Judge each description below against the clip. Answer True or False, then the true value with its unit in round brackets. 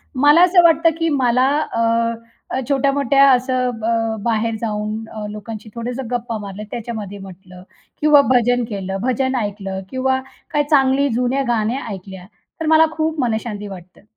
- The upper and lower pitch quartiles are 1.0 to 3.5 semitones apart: False (4.2 semitones)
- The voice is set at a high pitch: True (235 Hz)